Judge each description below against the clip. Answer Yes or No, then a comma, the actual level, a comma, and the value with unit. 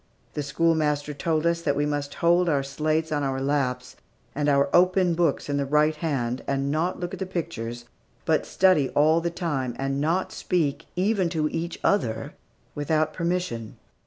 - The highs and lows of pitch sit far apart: No, average, 3.3 semitones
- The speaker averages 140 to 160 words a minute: No, average, 175 wpm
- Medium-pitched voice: Yes, medium, 150 Hz